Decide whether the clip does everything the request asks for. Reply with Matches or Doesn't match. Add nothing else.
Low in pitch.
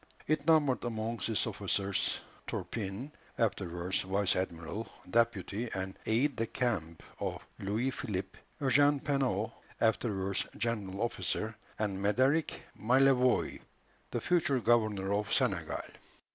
Matches